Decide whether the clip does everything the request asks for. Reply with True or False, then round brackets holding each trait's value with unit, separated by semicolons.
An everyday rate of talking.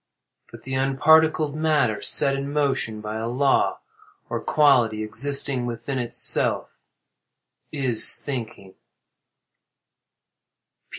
False (95 wpm)